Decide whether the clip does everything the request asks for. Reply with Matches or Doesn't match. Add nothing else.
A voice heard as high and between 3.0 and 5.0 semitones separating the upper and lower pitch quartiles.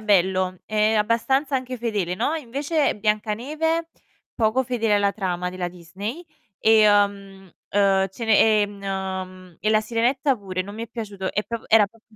Matches